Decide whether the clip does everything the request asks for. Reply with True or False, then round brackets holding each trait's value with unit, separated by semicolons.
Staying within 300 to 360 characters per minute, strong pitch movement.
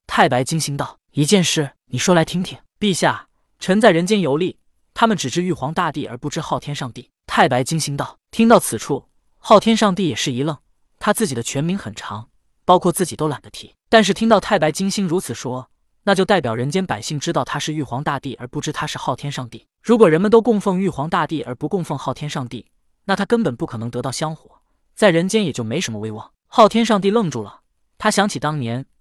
True (325 characters per minute; 6.9 semitones)